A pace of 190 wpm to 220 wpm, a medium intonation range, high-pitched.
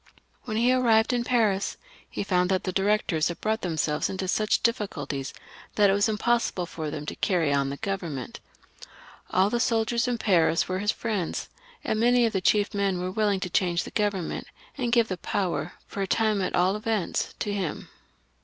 Yes: average, 200 wpm; average, 3.6 semitones; high, 200 Hz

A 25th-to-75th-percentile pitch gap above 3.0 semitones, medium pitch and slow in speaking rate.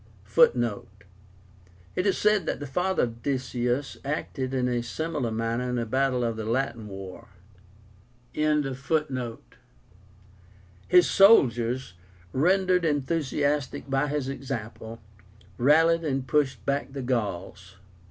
No: average, 4.5 semitones; low, 130 Hz; slow, 115 wpm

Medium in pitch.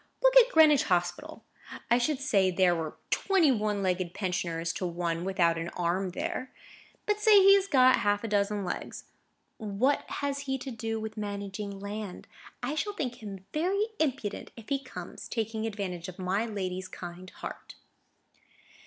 No: high, 210 Hz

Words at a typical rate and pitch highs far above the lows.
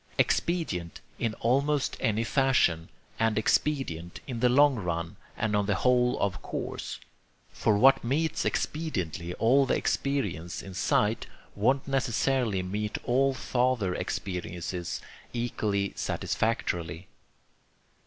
No: slow, 115 wpm; wide, 6.4 semitones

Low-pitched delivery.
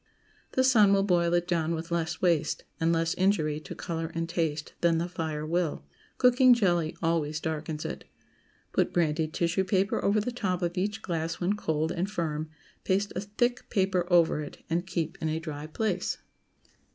No: medium, 170 Hz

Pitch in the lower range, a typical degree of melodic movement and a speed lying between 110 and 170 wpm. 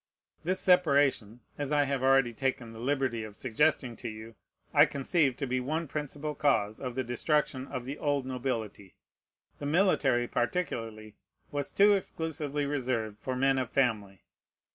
Yes: low, 130 Hz; average, 3.7 semitones; average, 155 wpm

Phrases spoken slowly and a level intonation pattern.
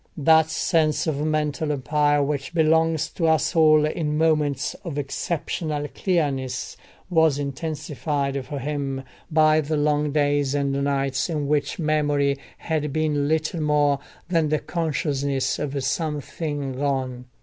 Yes: slow, 130 wpm; narrow, 1.8 semitones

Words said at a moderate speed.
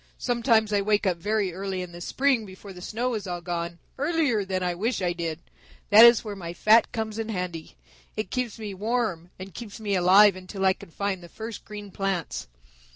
No: fast, 210 wpm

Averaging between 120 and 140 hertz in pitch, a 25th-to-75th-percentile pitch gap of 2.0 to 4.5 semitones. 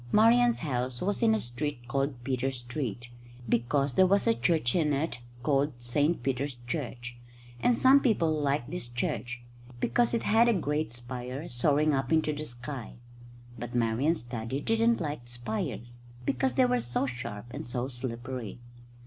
No: low, 135 Hz; average, 5.0 semitones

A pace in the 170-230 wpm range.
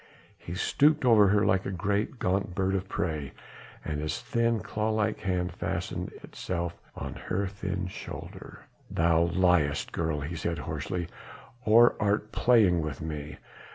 No: average, 150 wpm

